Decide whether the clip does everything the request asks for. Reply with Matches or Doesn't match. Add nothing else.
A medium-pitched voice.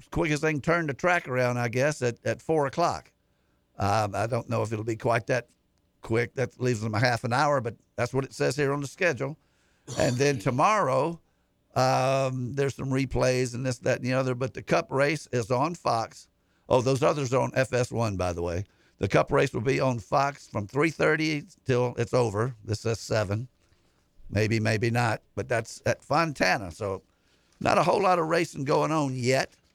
Doesn't match